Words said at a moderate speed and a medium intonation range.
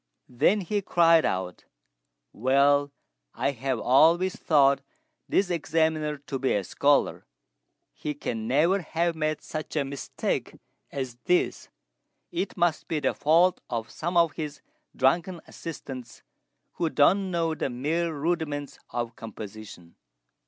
No: slow, 130 wpm; average, 4.3 semitones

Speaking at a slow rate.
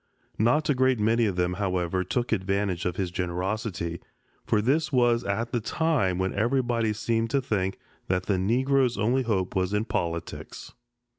No: average, 165 wpm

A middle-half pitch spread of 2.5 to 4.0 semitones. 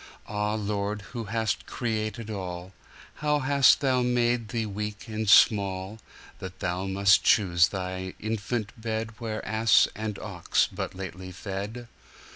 Yes: average, 2.8 semitones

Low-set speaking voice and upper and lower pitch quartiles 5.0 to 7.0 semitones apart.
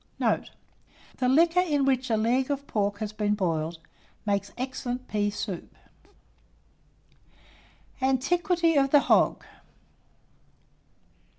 No: very high, 255 Hz; average, 5.3 semitones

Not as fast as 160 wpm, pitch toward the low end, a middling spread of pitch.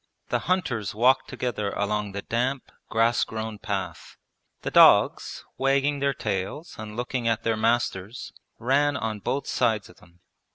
Yes: average, 150 wpm; low, 115 Hz; average, 3.9 semitones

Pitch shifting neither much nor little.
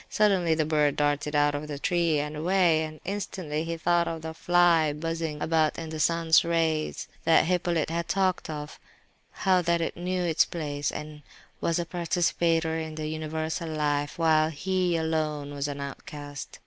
No: narrow, 2.1 semitones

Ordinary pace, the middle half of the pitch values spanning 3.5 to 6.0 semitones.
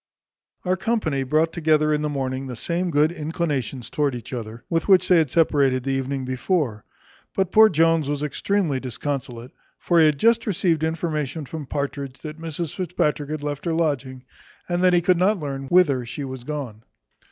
Yes: average, 185 wpm; average, 4.0 semitones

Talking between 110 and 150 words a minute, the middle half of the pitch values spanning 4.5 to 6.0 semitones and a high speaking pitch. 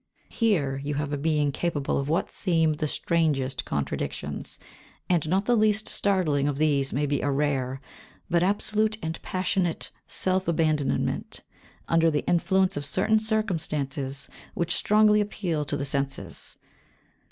No: average, 140 wpm; average, 4.9 semitones; medium, 160 Hz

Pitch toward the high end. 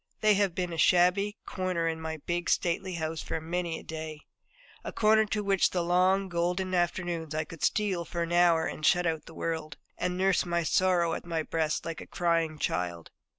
No: medium, 170 Hz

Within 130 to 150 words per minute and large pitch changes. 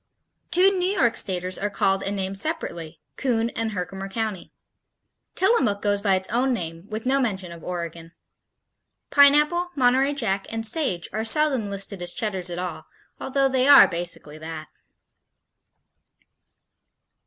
Yes: average, 140 wpm; wide, 6.5 semitones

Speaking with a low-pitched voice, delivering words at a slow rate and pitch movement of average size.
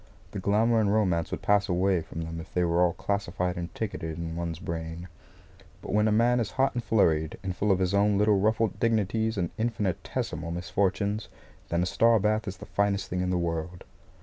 No: very low, 95 Hz; fast, 205 wpm; average, 3.7 semitones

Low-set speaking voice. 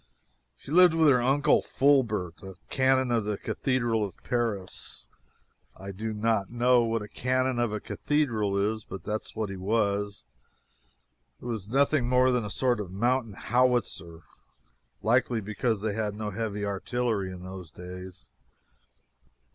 Yes: low, 110 Hz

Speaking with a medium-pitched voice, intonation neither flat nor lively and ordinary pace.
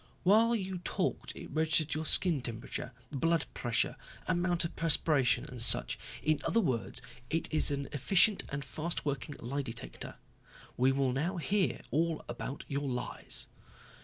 Yes: medium, 150 Hz; average, 4.2 semitones; average, 150 wpm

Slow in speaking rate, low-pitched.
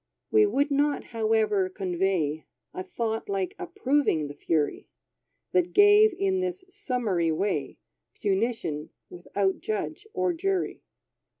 No: slow, 115 wpm; high, 230 Hz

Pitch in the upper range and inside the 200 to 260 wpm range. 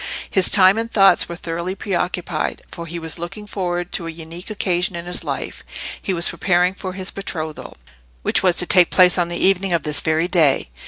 No: medium, 180 Hz; fast, 205 wpm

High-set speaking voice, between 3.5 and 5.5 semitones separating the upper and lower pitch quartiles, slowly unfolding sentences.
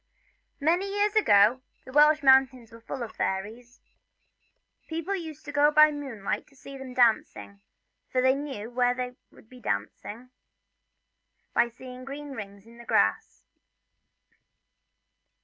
Yes: very high, 260 Hz; average, 4.2 semitones; slow, 130 wpm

